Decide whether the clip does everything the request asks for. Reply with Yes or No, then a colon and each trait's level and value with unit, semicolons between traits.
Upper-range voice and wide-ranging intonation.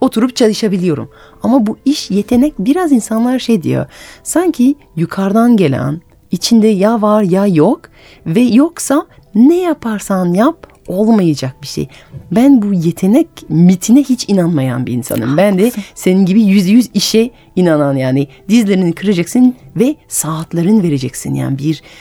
Yes: high, 205 Hz; wide, 6.1 semitones